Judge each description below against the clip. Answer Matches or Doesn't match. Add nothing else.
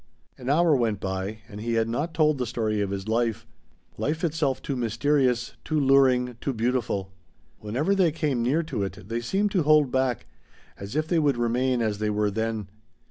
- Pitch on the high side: Doesn't match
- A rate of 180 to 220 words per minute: Matches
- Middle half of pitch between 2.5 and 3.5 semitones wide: Doesn't match